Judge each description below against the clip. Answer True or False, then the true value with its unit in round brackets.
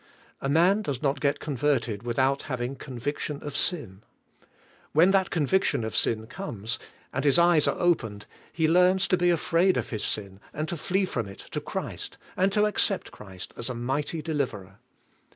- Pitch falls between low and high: True (145 Hz)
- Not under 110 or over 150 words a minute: False (175 wpm)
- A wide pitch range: True (6.7 semitones)